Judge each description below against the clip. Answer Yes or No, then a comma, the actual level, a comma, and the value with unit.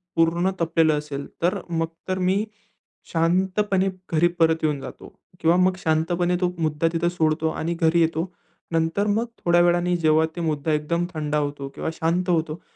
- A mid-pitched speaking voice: Yes, medium, 165 Hz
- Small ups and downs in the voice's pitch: Yes, narrow, 1.9 semitones